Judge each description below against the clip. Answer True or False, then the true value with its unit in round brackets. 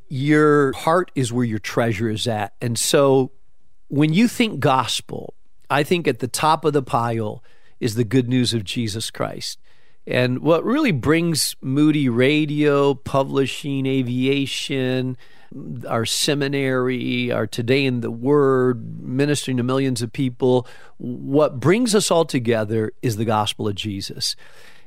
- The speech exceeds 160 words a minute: False (140 wpm)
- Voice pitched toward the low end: True (130 Hz)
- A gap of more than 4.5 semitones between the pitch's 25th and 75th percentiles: False (3.1 semitones)